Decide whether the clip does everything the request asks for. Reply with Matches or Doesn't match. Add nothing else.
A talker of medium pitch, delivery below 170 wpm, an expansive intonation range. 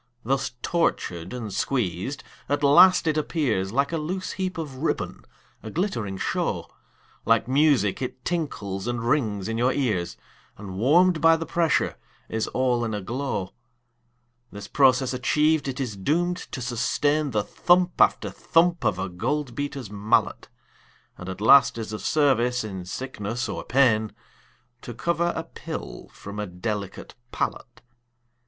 Doesn't match